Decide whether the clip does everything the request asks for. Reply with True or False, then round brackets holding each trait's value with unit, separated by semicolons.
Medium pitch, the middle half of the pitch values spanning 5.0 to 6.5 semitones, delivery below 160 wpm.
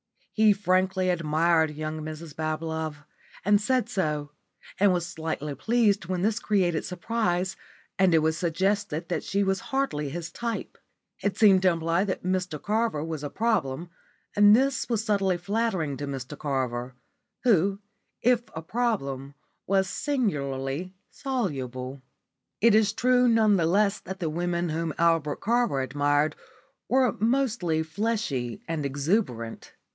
True (175 Hz; 5.3 semitones; 140 wpm)